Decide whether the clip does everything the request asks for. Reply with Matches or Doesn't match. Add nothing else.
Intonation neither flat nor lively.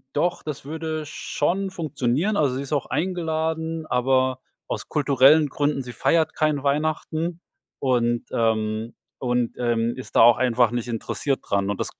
Matches